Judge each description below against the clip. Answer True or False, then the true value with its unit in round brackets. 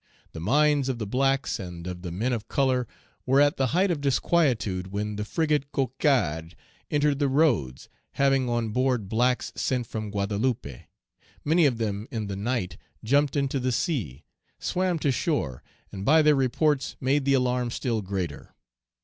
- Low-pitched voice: True (125 Hz)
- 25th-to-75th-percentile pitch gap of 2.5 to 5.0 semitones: False (5.4 semitones)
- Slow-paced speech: False (165 wpm)